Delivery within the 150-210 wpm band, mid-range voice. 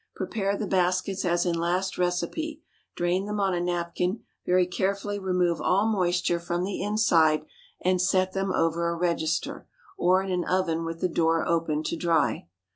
Yes: average, 170 wpm; medium, 180 Hz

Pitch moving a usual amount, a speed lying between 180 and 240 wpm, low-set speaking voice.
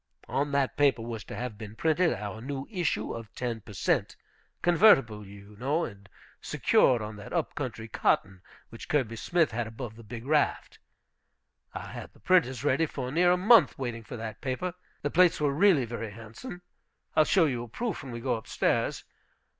No: wide, 5.7 semitones; average, 190 wpm; low, 125 Hz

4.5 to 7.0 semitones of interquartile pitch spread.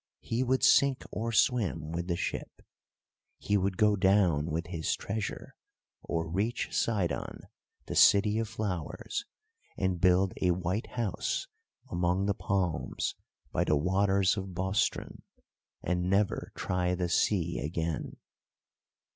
No: average, 3.0 semitones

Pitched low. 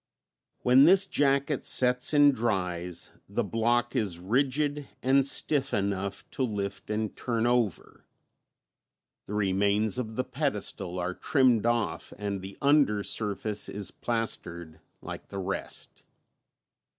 Yes: low, 110 Hz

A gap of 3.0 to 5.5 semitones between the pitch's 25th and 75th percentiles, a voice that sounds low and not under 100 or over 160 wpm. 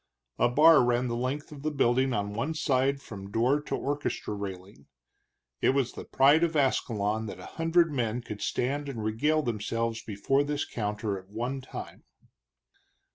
No: average, 4.9 semitones; low, 125 Hz; average, 170 wpm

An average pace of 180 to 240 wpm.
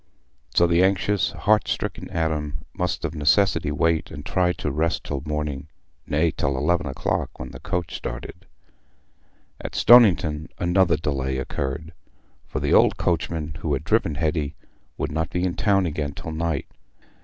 No: average, 155 wpm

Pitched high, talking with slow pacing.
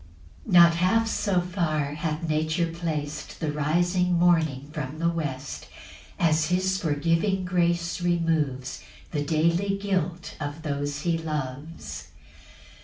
No: medium, 165 Hz; slow, 120 wpm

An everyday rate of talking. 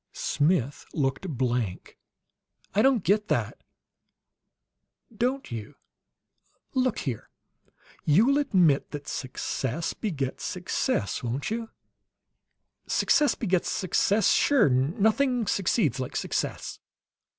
No: slow, 95 wpm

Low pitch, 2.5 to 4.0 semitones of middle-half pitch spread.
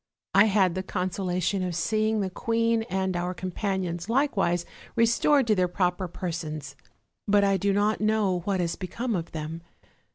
No: high, 190 Hz; average, 3.3 semitones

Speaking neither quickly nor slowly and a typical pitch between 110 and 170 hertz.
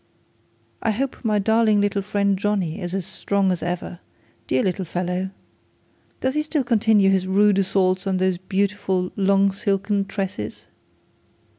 No: average, 145 wpm; high, 195 Hz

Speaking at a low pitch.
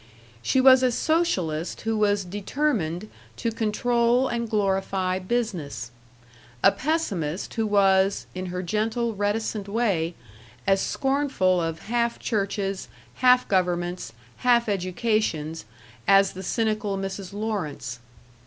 No: high, 205 Hz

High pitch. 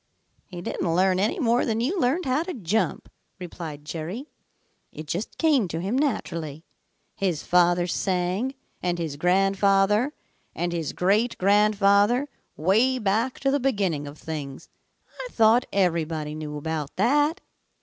Yes: high, 195 Hz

